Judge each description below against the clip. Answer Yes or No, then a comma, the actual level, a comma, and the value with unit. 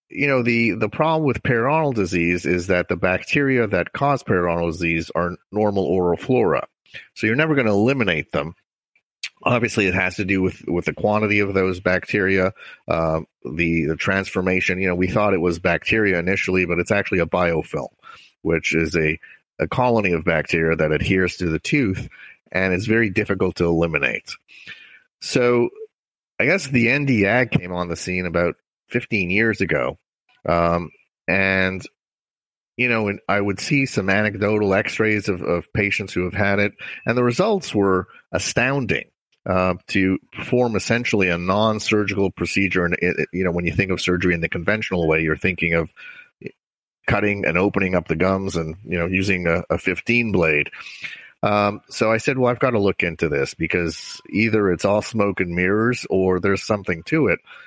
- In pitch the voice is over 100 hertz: No, very low, 95 Hz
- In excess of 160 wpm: Yes, average, 180 wpm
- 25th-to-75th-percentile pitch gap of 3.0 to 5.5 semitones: Yes, average, 3.7 semitones